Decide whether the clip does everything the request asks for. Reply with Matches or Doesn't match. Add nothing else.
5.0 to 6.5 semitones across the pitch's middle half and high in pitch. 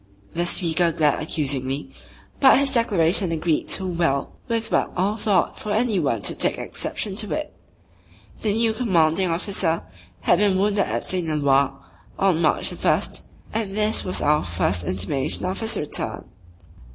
Doesn't match